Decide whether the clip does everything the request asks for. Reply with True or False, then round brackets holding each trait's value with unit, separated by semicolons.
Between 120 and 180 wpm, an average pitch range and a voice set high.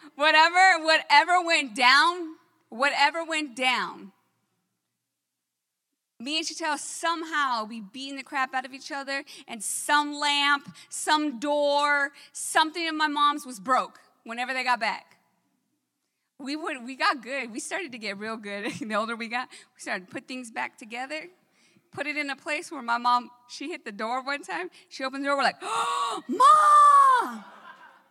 True (165 wpm; 4.0 semitones; 285 Hz)